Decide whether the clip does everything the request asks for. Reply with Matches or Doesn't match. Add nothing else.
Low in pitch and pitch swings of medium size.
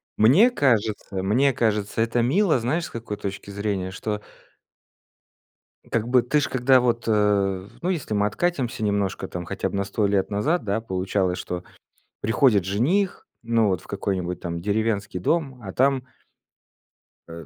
Matches